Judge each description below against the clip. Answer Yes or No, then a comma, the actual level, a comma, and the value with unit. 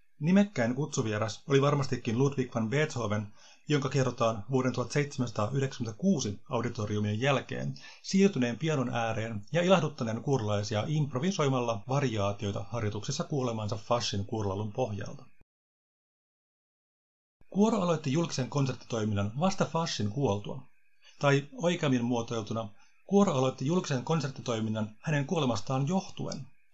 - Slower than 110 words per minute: Yes, slow, 95 wpm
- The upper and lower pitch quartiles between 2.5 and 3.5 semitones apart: No, average, 5.1 semitones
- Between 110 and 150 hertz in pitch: Yes, low, 125 Hz